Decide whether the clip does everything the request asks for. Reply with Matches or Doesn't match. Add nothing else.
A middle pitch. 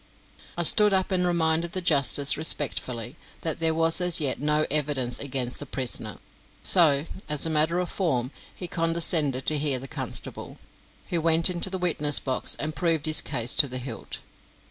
Matches